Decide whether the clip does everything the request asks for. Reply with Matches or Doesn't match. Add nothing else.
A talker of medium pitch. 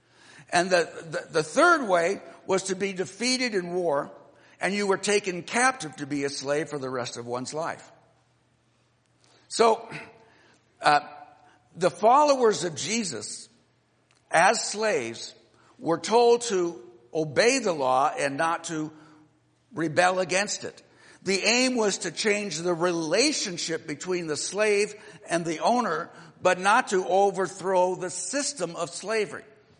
Matches